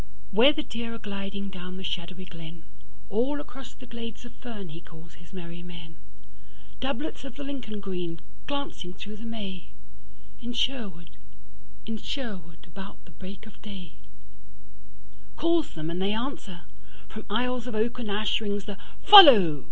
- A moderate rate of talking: Yes, average, 145 wpm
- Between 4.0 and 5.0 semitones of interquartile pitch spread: No, wide, 5.4 semitones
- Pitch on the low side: No, high, 200 Hz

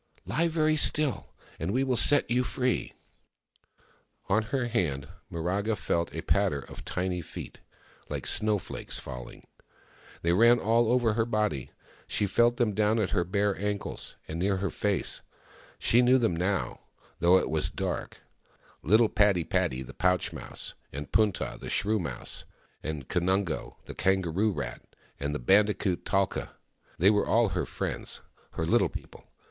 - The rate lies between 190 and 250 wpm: No, average, 160 wpm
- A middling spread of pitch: Yes, average, 4.6 semitones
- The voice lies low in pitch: Yes, low, 100 Hz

